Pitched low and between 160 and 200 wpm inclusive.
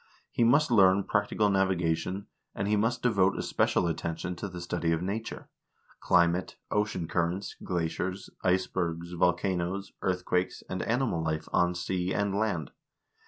No: very low, 90 Hz; average, 140 wpm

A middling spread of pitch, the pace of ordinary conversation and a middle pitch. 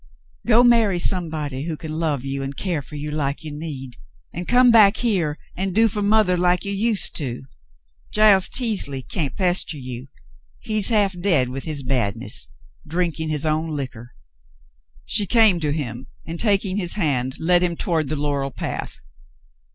No: wide, 6.1 semitones; average, 170 wpm; medium, 160 Hz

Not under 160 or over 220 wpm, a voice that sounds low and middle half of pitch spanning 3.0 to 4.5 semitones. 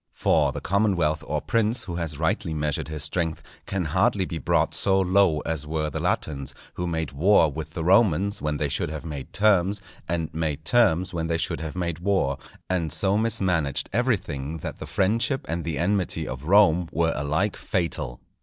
Yes: average, 185 wpm; very low, 85 Hz; average, 3.9 semitones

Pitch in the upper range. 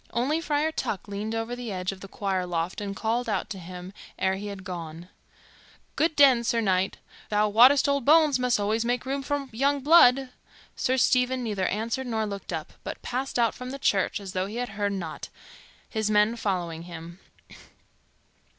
Yes: high, 220 Hz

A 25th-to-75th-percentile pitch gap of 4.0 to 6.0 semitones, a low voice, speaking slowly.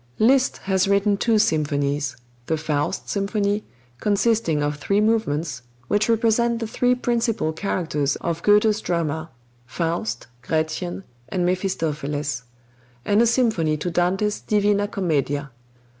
No: wide, 5.6 semitones; medium, 185 Hz; slow, 120 wpm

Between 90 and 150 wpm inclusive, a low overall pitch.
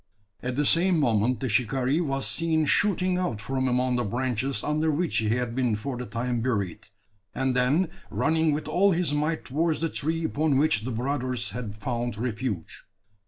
No: average, 180 wpm; low, 130 Hz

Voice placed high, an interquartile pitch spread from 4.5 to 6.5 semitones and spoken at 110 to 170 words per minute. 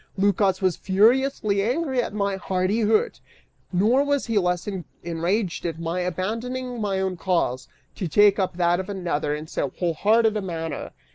No: high, 195 Hz; average, 3.7 semitones; average, 155 wpm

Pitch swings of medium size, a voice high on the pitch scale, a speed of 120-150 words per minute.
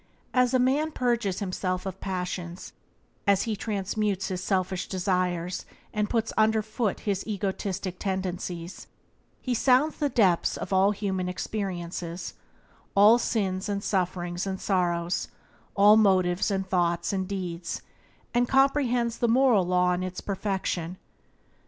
Yes: average, 3.2 semitones; high, 195 Hz; average, 140 wpm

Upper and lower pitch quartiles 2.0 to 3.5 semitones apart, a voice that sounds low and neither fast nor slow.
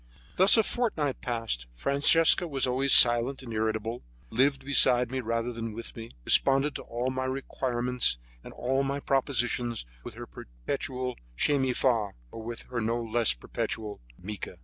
Yes: average, 2.9 semitones; low, 125 Hz; average, 160 wpm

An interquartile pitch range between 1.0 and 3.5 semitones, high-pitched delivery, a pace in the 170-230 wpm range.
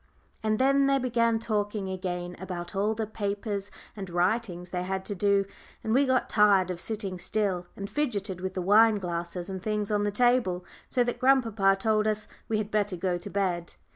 Yes: average, 3.0 semitones; high, 205 Hz; average, 195 wpm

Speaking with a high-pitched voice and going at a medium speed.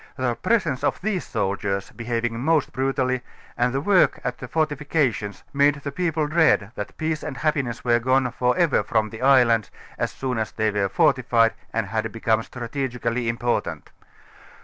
No: low, 125 Hz; average, 170 wpm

